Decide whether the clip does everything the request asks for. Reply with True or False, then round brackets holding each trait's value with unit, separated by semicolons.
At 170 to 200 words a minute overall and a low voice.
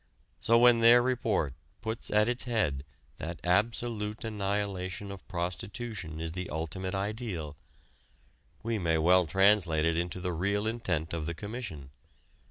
False (140 wpm; 95 Hz)